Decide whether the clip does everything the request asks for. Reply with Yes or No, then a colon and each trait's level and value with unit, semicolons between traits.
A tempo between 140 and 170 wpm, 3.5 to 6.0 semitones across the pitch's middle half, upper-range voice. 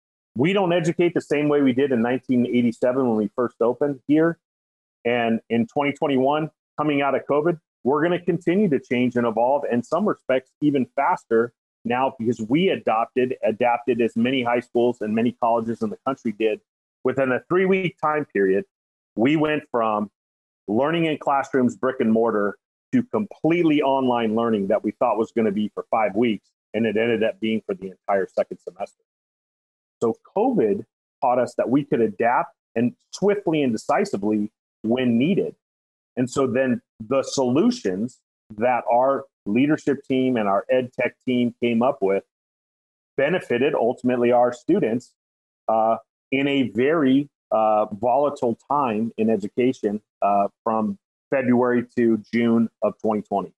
No: average, 160 wpm; average, 4.2 semitones; low, 125 Hz